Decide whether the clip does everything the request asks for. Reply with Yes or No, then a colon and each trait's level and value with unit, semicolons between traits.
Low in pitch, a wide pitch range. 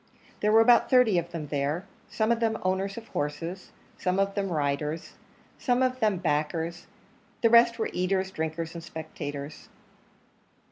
No: medium, 185 Hz; wide, 5.7 semitones